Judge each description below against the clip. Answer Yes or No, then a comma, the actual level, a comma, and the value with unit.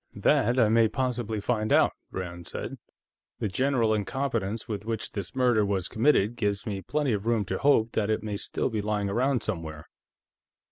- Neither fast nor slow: Yes, average, 180 wpm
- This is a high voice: No, low, 110 Hz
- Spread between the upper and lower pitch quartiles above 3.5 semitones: No, average, 3.0 semitones